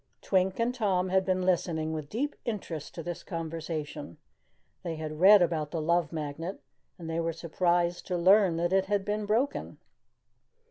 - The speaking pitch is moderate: Yes, medium, 175 Hz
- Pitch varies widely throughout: No, average, 2.9 semitones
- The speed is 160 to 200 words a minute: Yes, average, 170 wpm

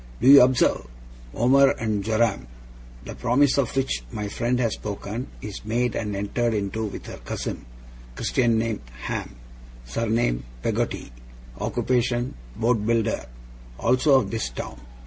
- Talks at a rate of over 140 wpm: No, slow, 135 wpm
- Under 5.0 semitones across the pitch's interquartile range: Yes, average, 2.8 semitones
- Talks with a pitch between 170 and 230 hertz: No, low, 115 Hz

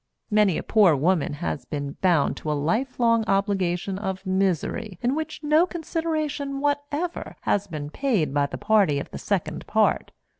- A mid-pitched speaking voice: No, high, 200 Hz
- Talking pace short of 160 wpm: No, average, 165 wpm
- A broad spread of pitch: Yes, wide, 8.4 semitones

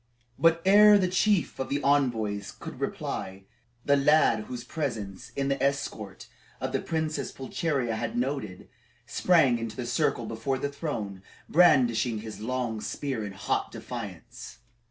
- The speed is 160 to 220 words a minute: No, average, 140 wpm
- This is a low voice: Yes, low, 130 Hz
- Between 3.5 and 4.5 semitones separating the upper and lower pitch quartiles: No, average, 4.9 semitones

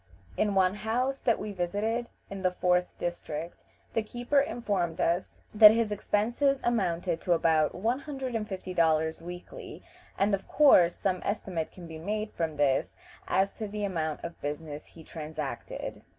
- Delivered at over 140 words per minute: Yes, average, 165 wpm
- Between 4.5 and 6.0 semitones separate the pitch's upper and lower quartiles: Yes, average, 4.8 semitones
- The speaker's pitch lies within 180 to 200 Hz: Yes, high, 190 Hz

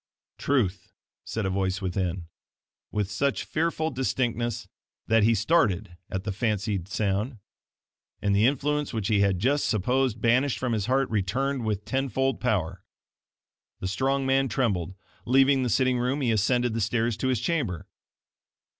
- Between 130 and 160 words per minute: Yes, average, 155 wpm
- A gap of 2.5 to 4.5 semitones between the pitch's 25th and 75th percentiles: No, average, 4.9 semitones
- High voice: No, low, 115 Hz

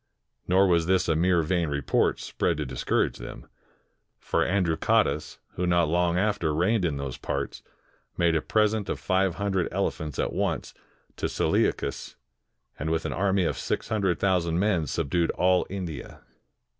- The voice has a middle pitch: No, very low, 90 Hz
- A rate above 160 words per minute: No, average, 155 wpm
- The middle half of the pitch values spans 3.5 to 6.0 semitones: No, average, 3.1 semitones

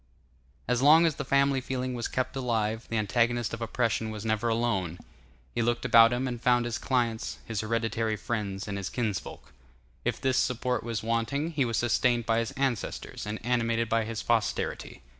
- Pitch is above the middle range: No, low, 115 Hz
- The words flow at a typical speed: Yes, average, 180 wpm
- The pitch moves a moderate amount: No, narrow, 2.0 semitones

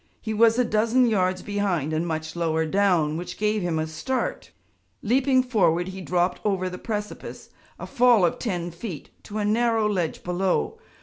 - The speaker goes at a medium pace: Yes, average, 175 wpm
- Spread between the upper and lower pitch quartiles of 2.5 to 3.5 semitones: No, average, 4.4 semitones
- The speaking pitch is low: No, high, 195 Hz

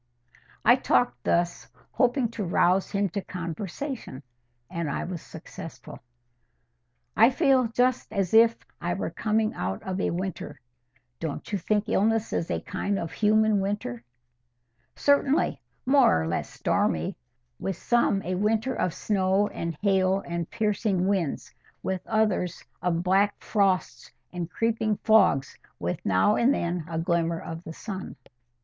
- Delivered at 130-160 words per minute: Yes, average, 140 wpm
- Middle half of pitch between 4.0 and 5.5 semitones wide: Yes, average, 4.3 semitones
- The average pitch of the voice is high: Yes, high, 195 Hz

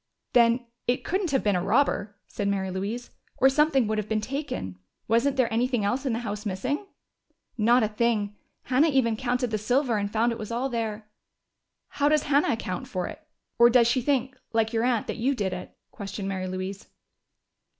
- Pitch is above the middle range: Yes, high, 230 Hz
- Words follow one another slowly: No, average, 195 wpm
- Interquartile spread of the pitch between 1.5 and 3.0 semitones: No, average, 3.7 semitones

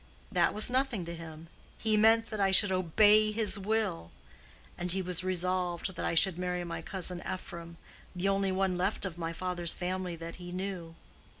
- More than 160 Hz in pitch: Yes, medium, 185 Hz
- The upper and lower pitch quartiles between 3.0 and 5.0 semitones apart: No, narrow, 2.5 semitones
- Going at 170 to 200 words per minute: Yes, average, 185 wpm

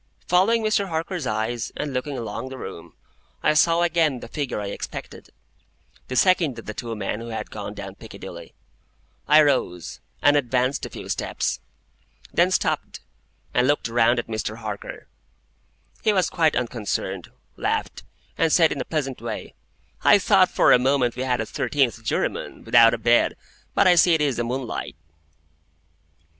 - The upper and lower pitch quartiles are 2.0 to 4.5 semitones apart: No, average, 5.1 semitones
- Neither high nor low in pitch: No, low, 125 Hz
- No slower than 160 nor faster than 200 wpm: Yes, average, 165 wpm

